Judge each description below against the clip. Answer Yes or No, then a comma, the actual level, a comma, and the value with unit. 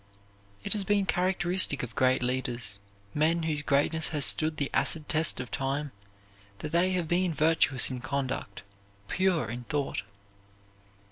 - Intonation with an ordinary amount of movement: Yes, average, 4.5 semitones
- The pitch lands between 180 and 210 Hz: No, medium, 150 Hz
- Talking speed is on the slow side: No, average, 145 wpm